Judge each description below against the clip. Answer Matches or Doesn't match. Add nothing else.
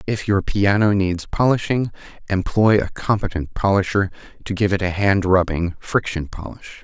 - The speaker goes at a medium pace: Matches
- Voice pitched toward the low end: Matches